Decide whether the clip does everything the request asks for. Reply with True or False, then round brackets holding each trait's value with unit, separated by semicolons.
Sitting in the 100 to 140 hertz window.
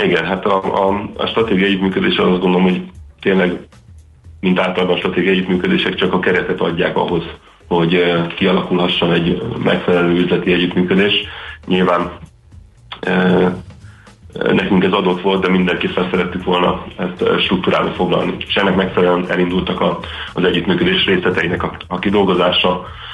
False (90 Hz)